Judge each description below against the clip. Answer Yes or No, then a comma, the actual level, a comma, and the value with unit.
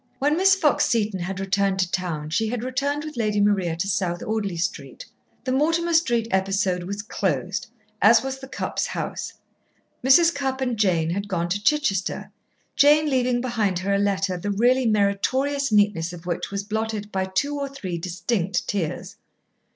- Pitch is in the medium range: No, high, 205 Hz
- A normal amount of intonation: No, wide, 5.7 semitones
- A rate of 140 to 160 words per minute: No, average, 175 wpm